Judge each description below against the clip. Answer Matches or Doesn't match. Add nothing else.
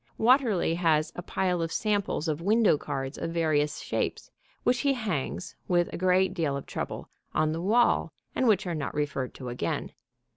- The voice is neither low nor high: Matches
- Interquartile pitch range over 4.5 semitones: Matches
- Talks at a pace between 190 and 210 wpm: Doesn't match